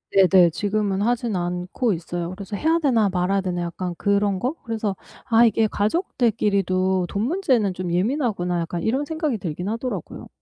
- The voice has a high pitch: Yes, high, 200 Hz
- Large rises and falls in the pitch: No, average, 4.4 semitones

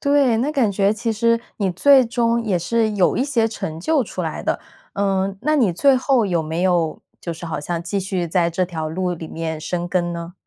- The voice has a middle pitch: No, high, 195 Hz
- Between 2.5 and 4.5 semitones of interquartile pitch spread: No, average, 5.2 semitones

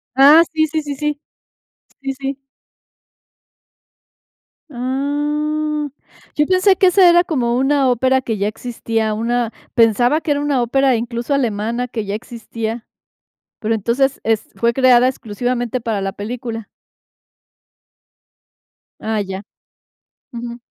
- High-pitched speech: Yes, high, 245 Hz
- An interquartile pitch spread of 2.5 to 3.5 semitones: No, average, 4.1 semitones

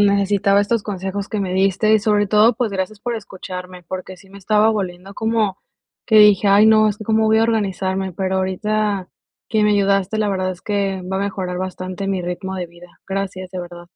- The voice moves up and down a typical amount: No, narrow, 2.1 semitones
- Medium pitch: No, high, 195 Hz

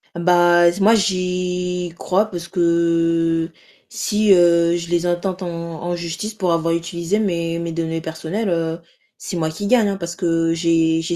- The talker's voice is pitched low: No, medium, 170 Hz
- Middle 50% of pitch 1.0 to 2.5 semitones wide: Yes, narrow, 1.6 semitones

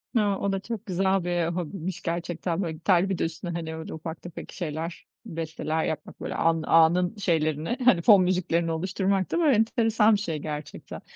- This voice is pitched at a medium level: Yes, medium, 175 Hz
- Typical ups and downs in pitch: Yes, average, 3.0 semitones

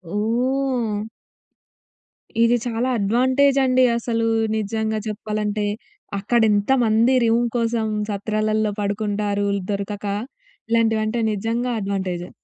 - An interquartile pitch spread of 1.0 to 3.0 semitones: Yes, narrow, 2.4 semitones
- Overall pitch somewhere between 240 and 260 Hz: No, high, 220 Hz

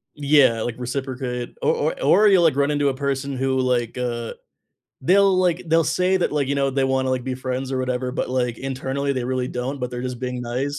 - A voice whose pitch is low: Yes, low, 130 Hz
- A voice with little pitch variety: Yes, narrow, 2.2 semitones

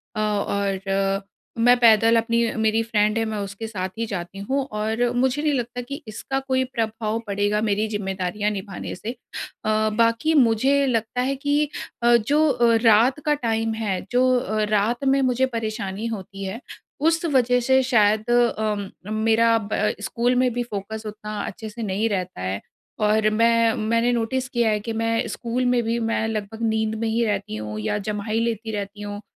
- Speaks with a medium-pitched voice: No, high, 220 Hz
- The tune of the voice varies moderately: No, narrow, 2.3 semitones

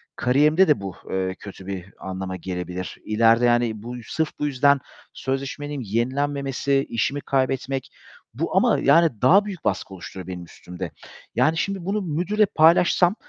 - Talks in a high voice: No, low, 130 Hz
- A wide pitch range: Yes, wide, 7.4 semitones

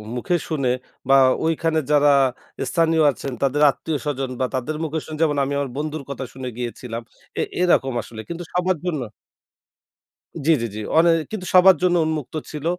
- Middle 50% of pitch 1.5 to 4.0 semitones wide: Yes, average, 3.4 semitones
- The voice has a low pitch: No, medium, 150 Hz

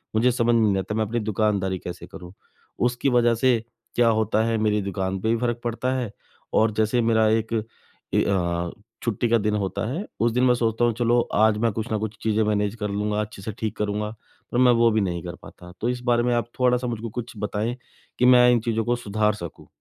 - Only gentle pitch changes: Yes, narrow, 2.3 semitones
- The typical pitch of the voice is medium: No, low, 110 Hz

